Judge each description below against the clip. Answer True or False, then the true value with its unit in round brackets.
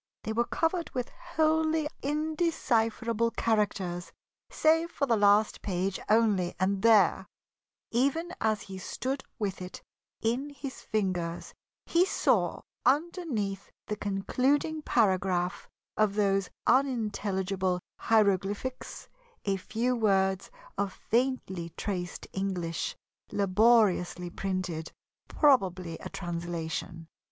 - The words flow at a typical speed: False (100 wpm)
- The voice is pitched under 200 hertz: False (210 Hz)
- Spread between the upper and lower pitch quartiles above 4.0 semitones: True (5.4 semitones)